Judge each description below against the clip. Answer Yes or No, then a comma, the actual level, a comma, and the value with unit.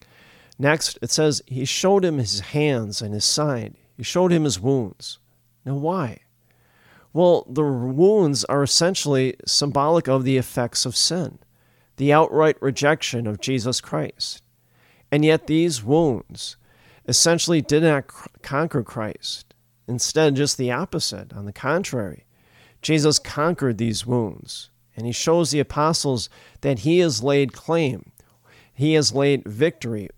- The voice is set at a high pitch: No, low, 135 Hz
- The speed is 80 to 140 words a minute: Yes, slow, 135 wpm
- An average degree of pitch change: Yes, average, 4.5 semitones